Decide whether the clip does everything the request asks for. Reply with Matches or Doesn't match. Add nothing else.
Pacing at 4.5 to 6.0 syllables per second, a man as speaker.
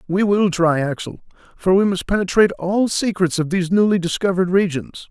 Matches